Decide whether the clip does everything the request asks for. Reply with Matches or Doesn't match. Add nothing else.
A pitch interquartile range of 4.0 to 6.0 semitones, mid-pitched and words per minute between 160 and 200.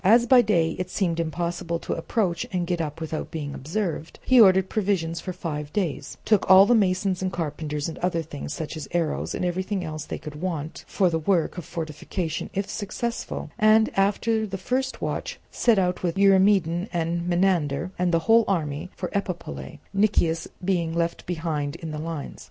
Doesn't match